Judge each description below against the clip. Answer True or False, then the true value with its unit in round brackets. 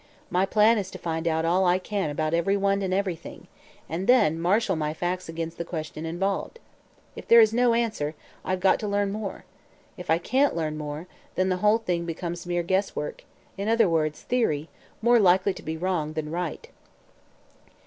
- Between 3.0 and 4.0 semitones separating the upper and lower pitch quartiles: True (3.7 semitones)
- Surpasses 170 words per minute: True (185 wpm)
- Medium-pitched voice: True (180 Hz)